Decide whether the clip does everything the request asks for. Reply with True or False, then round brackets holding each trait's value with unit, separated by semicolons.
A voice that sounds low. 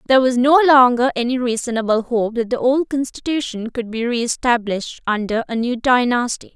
False (245 Hz)